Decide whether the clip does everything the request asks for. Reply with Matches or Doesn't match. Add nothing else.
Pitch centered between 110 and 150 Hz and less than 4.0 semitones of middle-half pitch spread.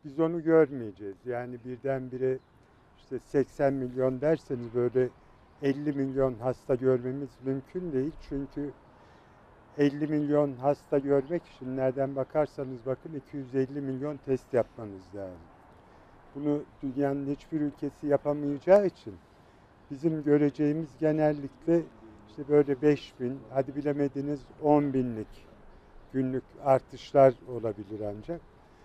Matches